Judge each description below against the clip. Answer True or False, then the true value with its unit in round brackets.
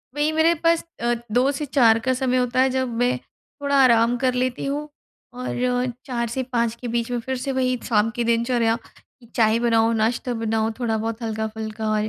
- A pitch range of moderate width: False (2.2 semitones)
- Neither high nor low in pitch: False (240 Hz)